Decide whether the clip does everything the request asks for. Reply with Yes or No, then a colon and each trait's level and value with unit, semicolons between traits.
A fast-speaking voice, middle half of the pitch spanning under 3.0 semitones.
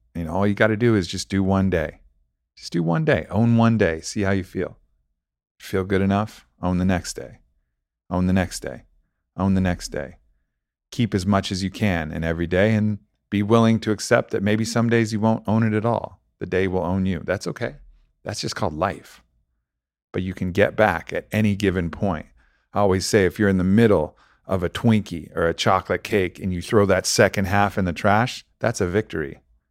No: fast, 220 wpm; average, 3.6 semitones